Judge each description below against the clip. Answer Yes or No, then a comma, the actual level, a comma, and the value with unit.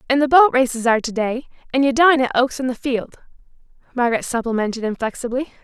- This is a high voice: Yes, very high, 250 Hz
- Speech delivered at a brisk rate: No, average, 190 wpm